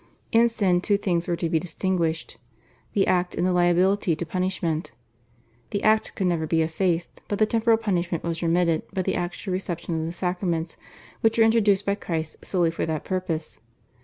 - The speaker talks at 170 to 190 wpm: Yes, average, 185 wpm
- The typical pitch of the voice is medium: Yes, medium, 180 Hz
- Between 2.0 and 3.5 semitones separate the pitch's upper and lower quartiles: Yes, average, 2.9 semitones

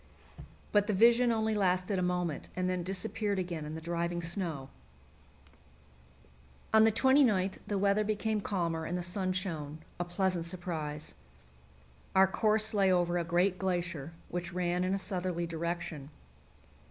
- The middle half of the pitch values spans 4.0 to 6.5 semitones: No, average, 2.8 semitones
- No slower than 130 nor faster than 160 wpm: Yes, average, 150 wpm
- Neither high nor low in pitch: Yes, medium, 180 Hz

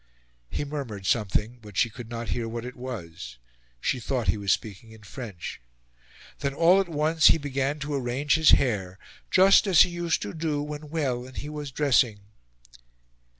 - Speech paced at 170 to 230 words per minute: Yes, average, 180 wpm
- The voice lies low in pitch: Yes, low, 130 Hz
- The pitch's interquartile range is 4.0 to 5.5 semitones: Yes, average, 5.2 semitones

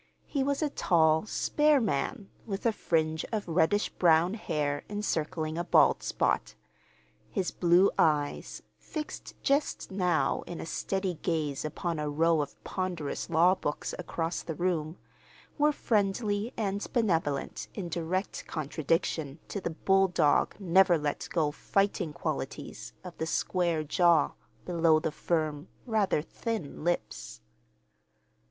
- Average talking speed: No, slow, 130 wpm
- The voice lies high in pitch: No, medium, 175 Hz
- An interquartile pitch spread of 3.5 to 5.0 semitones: Yes, average, 3.8 semitones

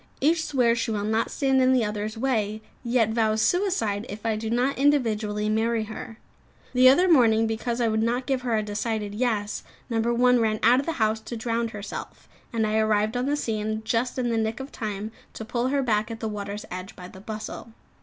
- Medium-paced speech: No, fast, 215 wpm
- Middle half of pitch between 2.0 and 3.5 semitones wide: Yes, narrow, 2.5 semitones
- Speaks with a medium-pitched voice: No, high, 225 Hz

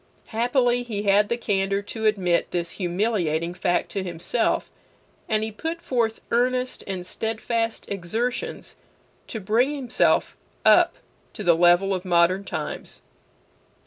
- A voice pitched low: No, high, 210 Hz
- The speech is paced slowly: Yes, slow, 130 wpm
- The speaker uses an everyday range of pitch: Yes, average, 4.6 semitones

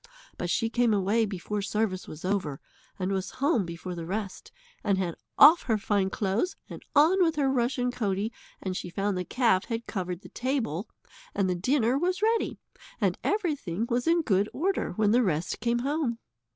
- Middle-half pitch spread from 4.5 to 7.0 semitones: Yes, wide, 5.6 semitones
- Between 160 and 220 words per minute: Yes, average, 185 wpm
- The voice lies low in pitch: No, high, 215 Hz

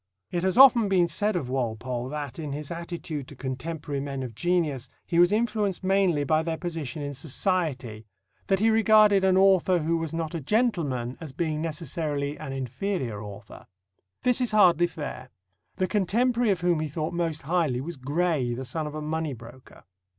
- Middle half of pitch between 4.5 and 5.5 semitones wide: Yes, average, 5.2 semitones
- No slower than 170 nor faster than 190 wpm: Yes, average, 180 wpm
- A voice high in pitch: No, medium, 160 Hz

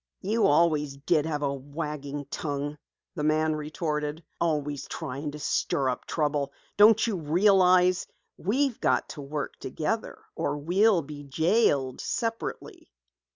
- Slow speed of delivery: Yes, slow, 130 wpm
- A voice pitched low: No, medium, 150 Hz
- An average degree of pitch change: Yes, average, 3.6 semitones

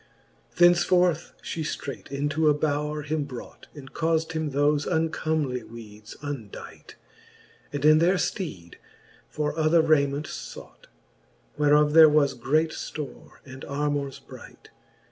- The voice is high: No, medium, 150 Hz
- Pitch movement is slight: Yes, narrow, 2.1 semitones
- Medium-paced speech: No, slow, 130 wpm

